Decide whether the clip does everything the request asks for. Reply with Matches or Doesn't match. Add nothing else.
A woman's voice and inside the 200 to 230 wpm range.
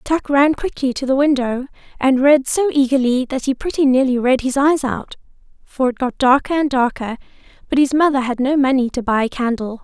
Matches